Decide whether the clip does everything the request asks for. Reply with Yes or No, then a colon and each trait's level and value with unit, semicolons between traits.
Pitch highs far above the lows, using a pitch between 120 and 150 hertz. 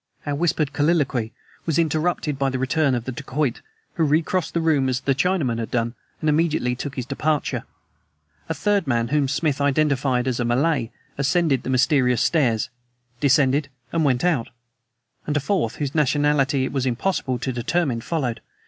No: average, 3.4 semitones; medium, 140 Hz